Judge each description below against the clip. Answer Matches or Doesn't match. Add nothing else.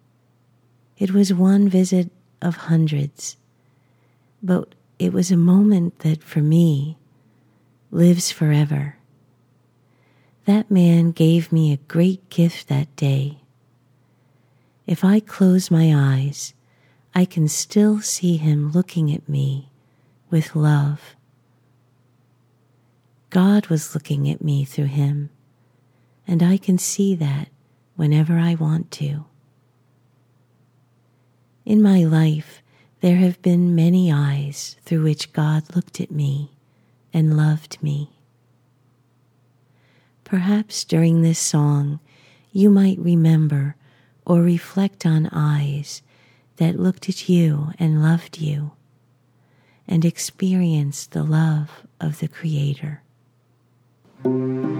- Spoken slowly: Matches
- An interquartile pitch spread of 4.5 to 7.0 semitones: Matches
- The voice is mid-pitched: Matches